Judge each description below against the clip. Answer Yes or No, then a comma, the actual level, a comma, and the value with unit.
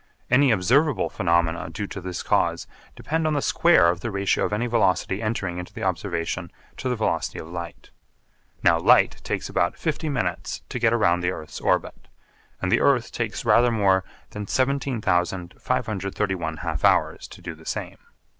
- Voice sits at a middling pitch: No, low, 100 Hz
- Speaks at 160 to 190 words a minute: Yes, average, 170 wpm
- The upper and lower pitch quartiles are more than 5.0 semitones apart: Yes, wide, 5.4 semitones